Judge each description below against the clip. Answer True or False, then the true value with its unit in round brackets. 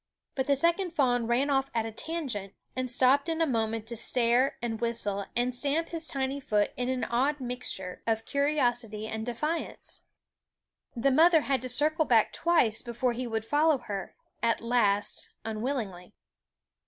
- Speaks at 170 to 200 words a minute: True (180 wpm)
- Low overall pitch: False (250 Hz)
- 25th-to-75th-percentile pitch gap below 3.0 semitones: False (3.9 semitones)